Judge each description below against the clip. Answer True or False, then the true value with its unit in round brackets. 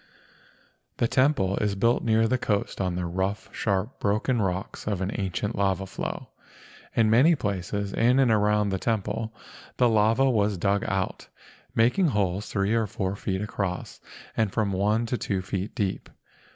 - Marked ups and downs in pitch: False (2.7 semitones)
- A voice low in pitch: True (105 Hz)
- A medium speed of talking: True (165 wpm)